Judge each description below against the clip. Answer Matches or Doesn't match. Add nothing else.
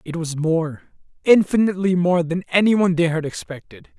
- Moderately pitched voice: Matches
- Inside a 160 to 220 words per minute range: Doesn't match